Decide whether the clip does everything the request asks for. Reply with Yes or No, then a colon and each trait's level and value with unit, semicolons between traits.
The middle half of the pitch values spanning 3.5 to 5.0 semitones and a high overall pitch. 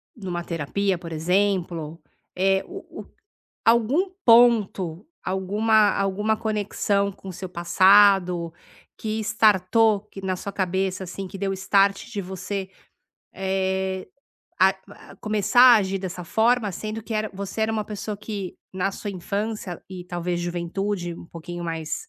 No: average, 2.8 semitones; high, 195 Hz